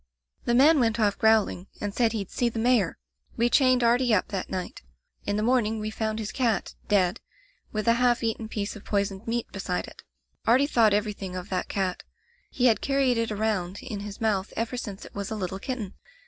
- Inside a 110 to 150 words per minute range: No, fast, 205 wpm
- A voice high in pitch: Yes, high, 220 Hz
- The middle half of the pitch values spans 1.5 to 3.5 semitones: Yes, average, 2.9 semitones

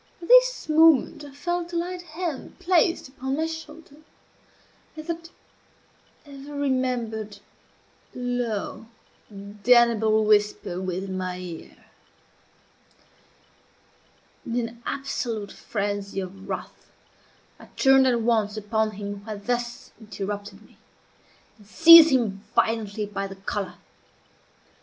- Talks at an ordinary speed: No, slow, 110 wpm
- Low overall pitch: No, high, 230 Hz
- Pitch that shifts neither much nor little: No, wide, 5.9 semitones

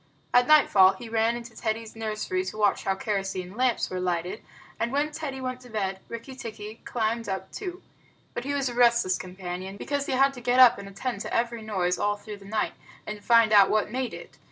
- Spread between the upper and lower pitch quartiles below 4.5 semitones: Yes, average, 3.9 semitones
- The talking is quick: Yes, fast, 215 wpm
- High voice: Yes, high, 220 Hz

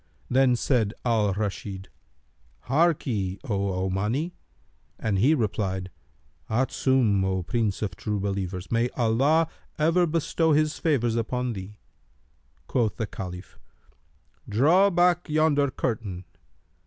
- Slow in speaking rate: Yes, slow, 110 wpm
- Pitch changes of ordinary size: No, wide, 6.5 semitones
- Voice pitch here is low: Yes, low, 115 Hz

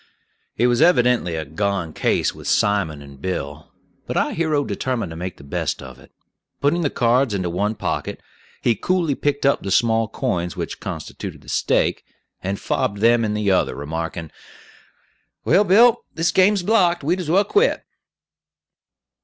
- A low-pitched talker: Yes, low, 115 Hz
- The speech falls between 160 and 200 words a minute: Yes, average, 165 wpm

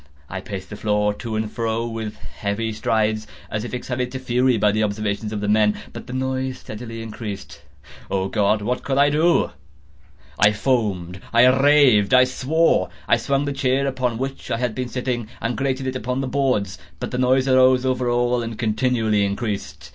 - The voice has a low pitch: Yes, low, 120 Hz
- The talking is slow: No, average, 180 wpm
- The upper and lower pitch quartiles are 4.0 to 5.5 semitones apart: No, average, 3.5 semitones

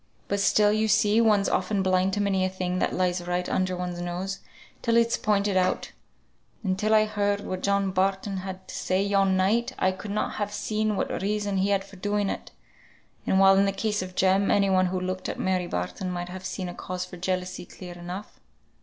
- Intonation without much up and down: Yes, narrow, 1.8 semitones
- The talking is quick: Yes, fast, 215 wpm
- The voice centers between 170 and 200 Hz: Yes, high, 190 Hz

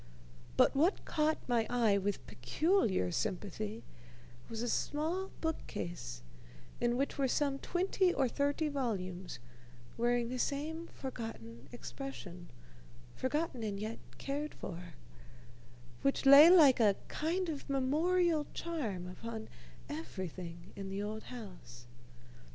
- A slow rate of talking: Yes, slow, 115 wpm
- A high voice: Yes, high, 240 Hz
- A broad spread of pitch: Yes, wide, 7.5 semitones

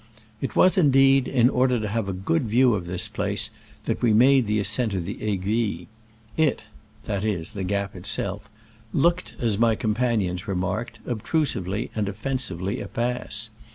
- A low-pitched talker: Yes, low, 110 Hz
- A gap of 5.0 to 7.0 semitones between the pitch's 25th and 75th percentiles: No, average, 4.1 semitones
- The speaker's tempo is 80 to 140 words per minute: No, average, 160 wpm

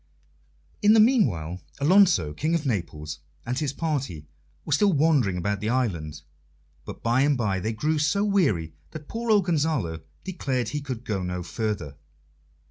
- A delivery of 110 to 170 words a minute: Yes, average, 160 wpm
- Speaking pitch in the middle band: No, low, 130 Hz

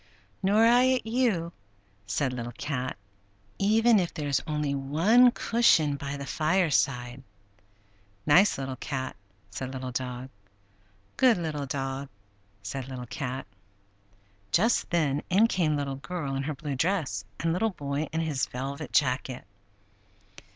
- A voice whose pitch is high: No, medium, 145 Hz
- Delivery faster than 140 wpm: No, slow, 135 wpm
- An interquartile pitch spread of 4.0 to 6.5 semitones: Yes, wide, 5.4 semitones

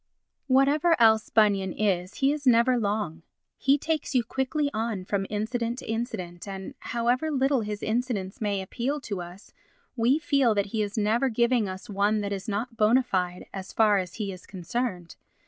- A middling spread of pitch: Yes, average, 4.2 semitones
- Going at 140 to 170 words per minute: No, average, 180 wpm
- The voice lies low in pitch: No, high, 220 Hz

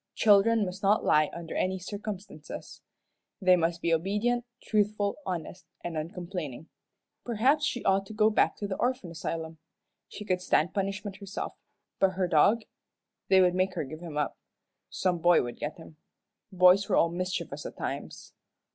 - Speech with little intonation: No, average, 3.4 semitones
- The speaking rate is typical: Yes, average, 165 wpm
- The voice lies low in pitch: No, medium, 185 Hz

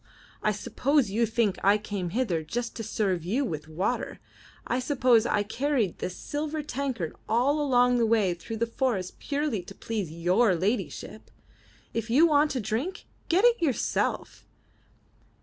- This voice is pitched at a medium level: No, high, 230 Hz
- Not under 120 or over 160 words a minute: Yes, average, 155 wpm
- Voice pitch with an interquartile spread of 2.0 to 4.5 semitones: No, wide, 5.5 semitones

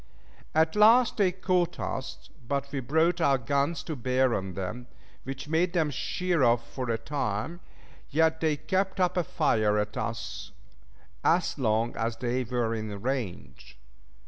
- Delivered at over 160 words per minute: No, average, 155 wpm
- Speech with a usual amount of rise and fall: No, wide, 6.1 semitones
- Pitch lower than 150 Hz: Yes, low, 135 Hz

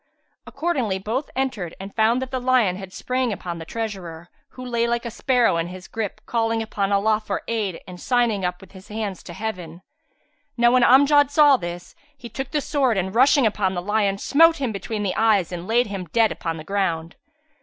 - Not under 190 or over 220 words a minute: Yes, average, 200 wpm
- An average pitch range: Yes, average, 4.7 semitones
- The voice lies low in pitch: No, high, 220 Hz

